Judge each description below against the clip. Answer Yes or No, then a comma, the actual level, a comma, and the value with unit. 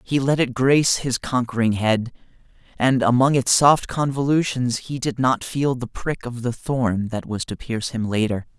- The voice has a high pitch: No, low, 125 Hz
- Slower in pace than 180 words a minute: No, average, 190 wpm